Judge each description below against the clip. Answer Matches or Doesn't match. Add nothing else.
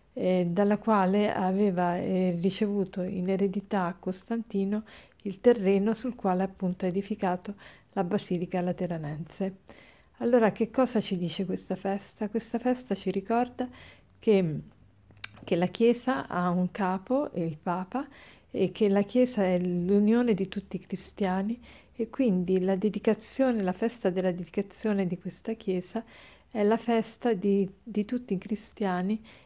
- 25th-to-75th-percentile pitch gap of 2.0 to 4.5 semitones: Matches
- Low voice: Doesn't match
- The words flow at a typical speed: Matches